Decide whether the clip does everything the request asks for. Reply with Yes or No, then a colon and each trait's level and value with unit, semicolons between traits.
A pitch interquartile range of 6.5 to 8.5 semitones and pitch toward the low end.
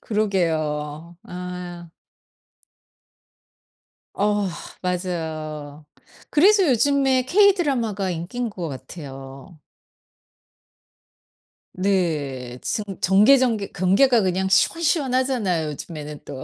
No: wide, 7.5 semitones; medium, 185 Hz